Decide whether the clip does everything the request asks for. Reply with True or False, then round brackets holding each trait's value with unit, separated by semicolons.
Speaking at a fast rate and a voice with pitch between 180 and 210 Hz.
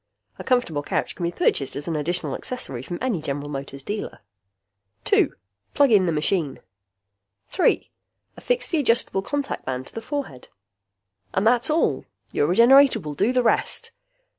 False (160 wpm; 190 Hz)